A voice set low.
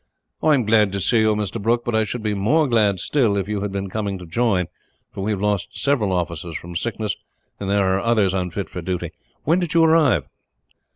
Yes: low, 105 Hz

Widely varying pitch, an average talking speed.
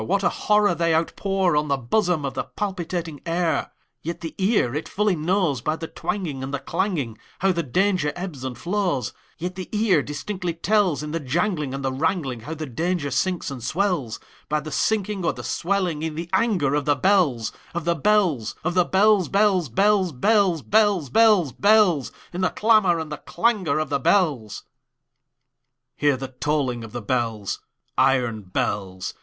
Yes: wide, 5.9 semitones; average, 150 wpm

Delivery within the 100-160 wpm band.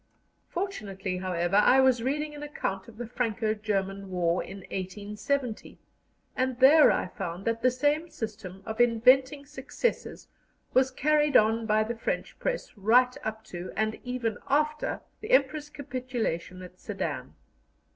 Yes: average, 145 wpm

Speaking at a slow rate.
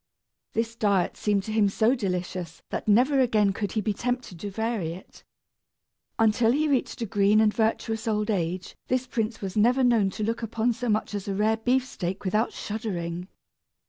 No: average, 180 wpm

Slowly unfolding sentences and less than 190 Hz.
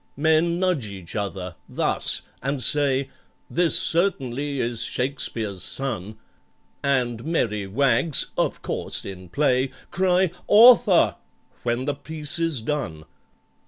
Yes: slow, 105 wpm; low, 135 Hz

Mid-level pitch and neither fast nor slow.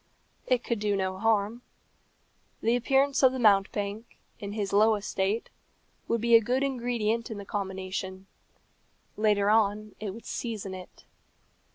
No: high, 215 Hz; average, 145 wpm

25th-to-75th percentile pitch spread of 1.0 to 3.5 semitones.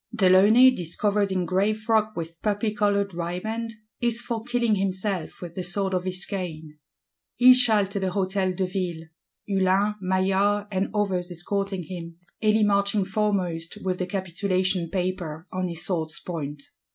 Yes: narrow, 2.5 semitones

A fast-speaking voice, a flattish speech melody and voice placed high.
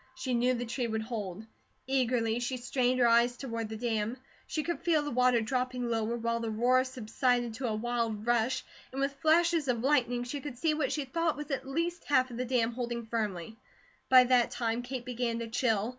Yes: fast, 210 wpm; narrow, 2.2 semitones; high, 245 Hz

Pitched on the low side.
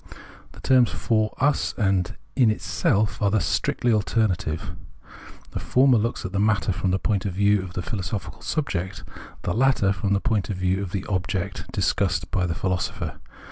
Yes: low, 100 Hz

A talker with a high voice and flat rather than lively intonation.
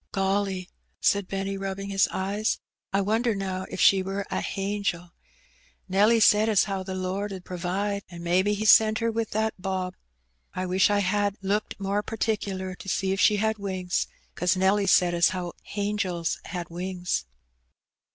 Yes: high, 195 Hz; narrow, 1.8 semitones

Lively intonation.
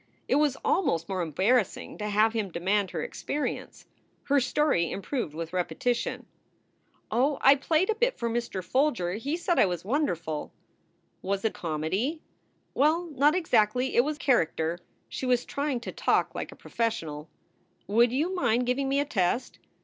Yes: wide, 7.4 semitones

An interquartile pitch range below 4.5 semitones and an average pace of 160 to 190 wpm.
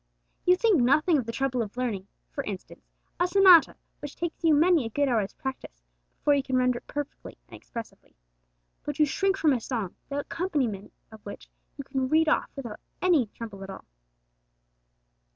No: wide, 5.4 semitones; average, 185 wpm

